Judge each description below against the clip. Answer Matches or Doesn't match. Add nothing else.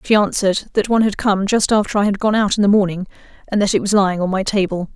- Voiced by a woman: Matches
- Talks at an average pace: Doesn't match